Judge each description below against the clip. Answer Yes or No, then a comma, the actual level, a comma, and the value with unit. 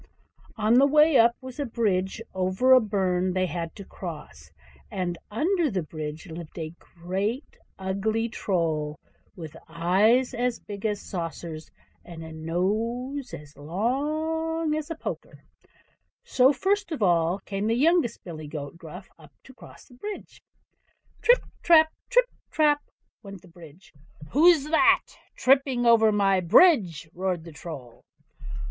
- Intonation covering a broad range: Yes, wide, 7.6 semitones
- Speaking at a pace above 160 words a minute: No, average, 140 wpm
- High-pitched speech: Yes, high, 200 Hz